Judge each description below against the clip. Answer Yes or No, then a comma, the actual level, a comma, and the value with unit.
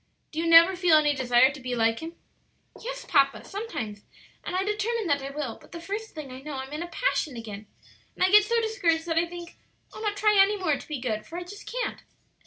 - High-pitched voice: Yes, very high, 330 Hz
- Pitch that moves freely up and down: Yes, wide, 6.9 semitones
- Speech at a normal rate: No, fast, 240 wpm